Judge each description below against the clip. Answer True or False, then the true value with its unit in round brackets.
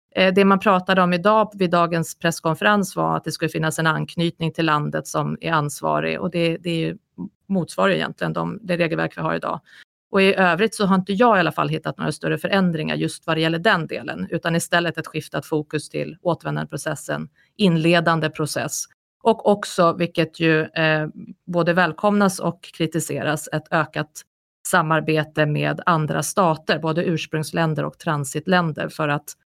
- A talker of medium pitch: True (165 Hz)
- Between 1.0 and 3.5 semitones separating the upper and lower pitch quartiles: True (2.9 semitones)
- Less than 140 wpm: False (165 wpm)